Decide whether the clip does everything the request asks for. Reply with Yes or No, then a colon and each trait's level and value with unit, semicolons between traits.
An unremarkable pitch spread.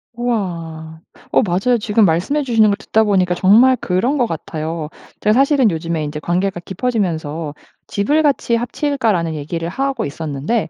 No: wide, 6.5 semitones